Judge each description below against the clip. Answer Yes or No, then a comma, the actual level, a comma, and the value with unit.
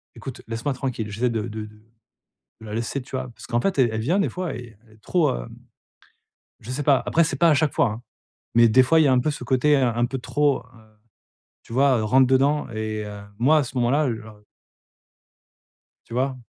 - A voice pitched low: Yes, low, 125 Hz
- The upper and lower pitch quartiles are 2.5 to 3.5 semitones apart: No, average, 3.9 semitones